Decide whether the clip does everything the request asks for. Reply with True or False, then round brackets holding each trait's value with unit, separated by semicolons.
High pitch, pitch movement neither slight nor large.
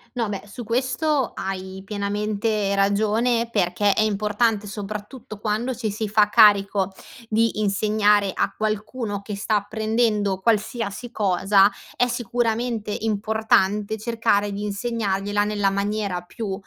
False (210 Hz; 2.0 semitones)